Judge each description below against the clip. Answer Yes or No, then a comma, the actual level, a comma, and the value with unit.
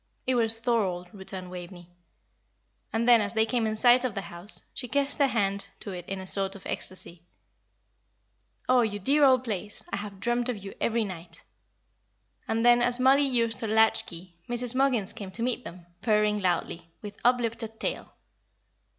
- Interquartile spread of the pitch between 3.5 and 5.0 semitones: Yes, average, 4.0 semitones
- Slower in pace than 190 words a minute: Yes, average, 180 wpm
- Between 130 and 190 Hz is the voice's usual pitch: No, high, 220 Hz